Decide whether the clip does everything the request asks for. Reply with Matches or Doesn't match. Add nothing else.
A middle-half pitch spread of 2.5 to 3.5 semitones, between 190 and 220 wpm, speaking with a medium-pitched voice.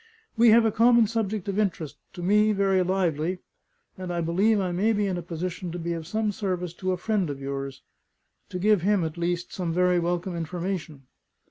Matches